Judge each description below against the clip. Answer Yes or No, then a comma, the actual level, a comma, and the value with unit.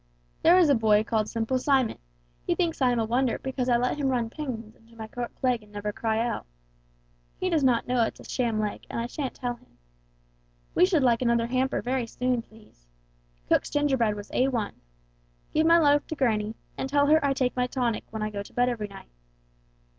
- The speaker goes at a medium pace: No, fast, 215 wpm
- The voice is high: Yes, high, 245 Hz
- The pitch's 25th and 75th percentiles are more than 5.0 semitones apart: No, average, 3.1 semitones